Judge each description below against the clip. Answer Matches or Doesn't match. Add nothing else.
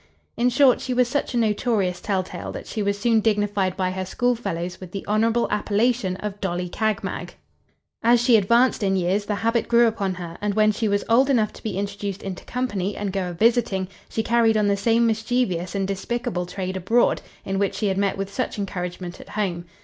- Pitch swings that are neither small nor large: Matches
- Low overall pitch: Doesn't match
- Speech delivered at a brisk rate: Matches